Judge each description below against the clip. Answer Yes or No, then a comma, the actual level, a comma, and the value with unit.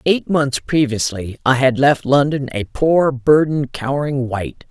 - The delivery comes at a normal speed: Yes, average, 155 wpm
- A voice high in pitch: No, low, 135 Hz